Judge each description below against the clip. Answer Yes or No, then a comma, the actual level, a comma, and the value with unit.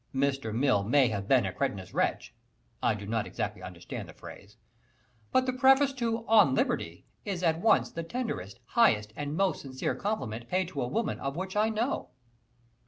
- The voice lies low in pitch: No, medium, 145 Hz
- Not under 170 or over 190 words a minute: Yes, average, 180 wpm